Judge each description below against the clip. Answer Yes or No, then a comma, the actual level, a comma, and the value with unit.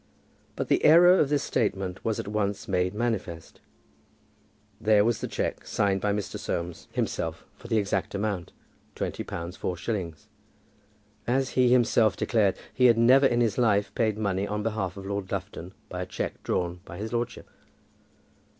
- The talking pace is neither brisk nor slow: Yes, average, 170 wpm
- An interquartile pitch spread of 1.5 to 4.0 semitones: Yes, average, 3.5 semitones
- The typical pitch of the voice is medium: No, low, 105 Hz